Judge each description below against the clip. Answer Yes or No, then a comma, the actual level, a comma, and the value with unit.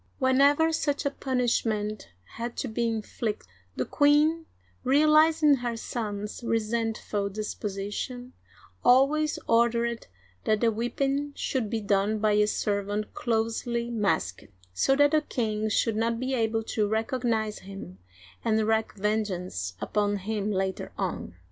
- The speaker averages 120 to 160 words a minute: Yes, average, 140 wpm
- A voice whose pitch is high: Yes, high, 225 Hz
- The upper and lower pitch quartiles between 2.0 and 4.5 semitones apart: Yes, average, 3.4 semitones